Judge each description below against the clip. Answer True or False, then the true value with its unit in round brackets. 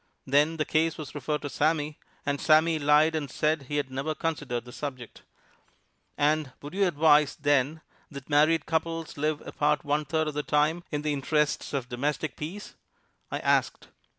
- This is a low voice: False (150 Hz)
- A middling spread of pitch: False (1.5 semitones)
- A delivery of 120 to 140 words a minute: False (175 wpm)